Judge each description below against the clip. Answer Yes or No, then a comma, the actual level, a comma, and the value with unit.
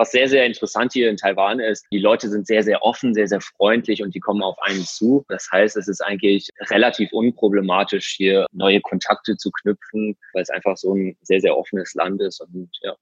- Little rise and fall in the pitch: Yes, narrow, 2.1 semitones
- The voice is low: Yes, low, 105 Hz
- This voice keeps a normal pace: No, fast, 220 wpm